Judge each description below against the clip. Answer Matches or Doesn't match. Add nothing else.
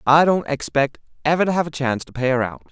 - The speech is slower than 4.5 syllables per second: Doesn't match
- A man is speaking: Matches